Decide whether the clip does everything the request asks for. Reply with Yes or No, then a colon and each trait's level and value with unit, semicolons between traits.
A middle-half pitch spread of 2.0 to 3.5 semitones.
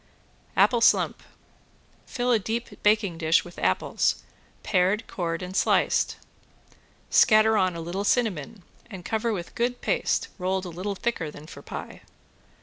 No: average, 4.3 semitones